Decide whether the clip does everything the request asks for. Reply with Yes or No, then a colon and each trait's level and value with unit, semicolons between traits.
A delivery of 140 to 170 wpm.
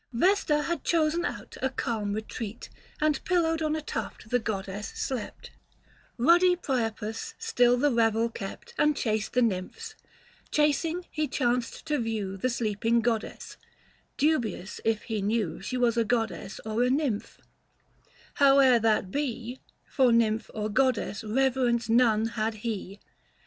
Yes: average, 145 wpm